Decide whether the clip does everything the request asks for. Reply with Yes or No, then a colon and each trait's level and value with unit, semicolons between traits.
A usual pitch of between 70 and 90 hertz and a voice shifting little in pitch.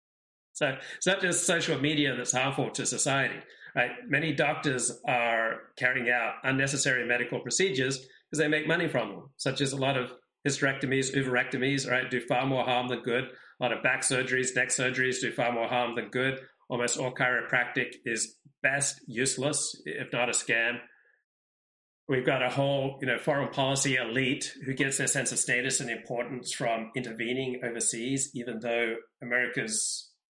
No: low, 130 Hz; narrow, 2.0 semitones